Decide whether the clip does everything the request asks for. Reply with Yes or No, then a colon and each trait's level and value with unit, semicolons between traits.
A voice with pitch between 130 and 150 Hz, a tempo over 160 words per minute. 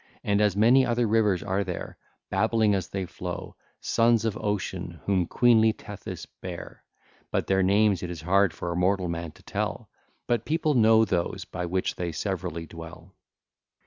No: very low, 95 Hz; average, 175 wpm